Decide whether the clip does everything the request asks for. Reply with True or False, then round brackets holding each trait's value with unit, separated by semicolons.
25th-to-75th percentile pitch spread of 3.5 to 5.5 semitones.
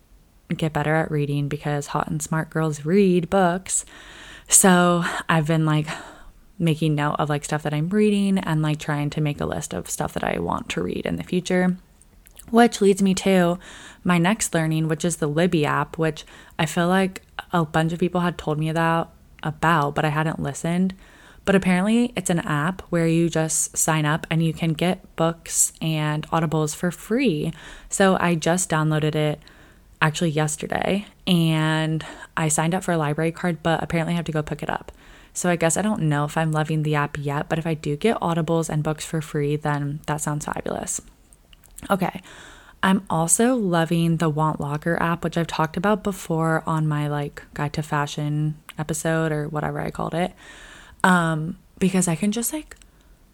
False (2.6 semitones)